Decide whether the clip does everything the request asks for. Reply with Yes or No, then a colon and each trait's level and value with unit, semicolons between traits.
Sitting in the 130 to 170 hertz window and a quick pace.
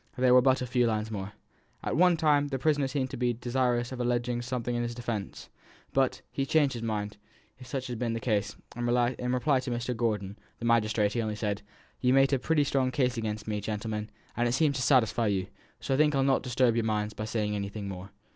No: low, 120 Hz; fast, 240 wpm